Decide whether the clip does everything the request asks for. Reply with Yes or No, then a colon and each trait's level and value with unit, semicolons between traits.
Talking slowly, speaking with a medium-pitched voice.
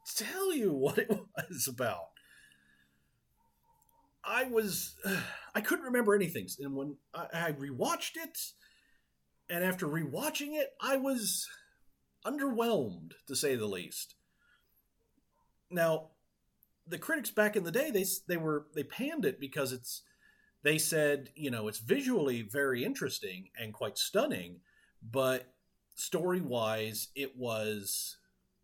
Yes: slow, 130 wpm; medium, 170 Hz